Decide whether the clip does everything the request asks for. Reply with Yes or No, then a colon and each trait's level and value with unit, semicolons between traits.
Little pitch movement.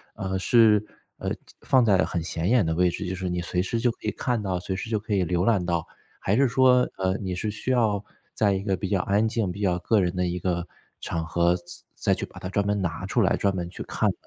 No: average, 3.2 semitones